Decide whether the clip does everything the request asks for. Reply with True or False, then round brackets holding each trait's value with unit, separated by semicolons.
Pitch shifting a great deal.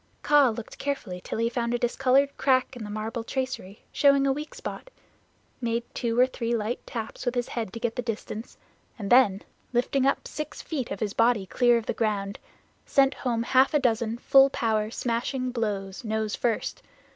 False (3.1 semitones)